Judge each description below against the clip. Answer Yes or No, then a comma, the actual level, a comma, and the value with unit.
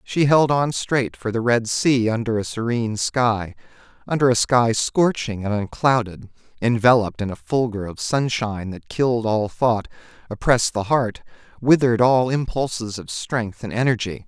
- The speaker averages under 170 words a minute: Yes, average, 160 wpm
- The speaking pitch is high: No, low, 115 Hz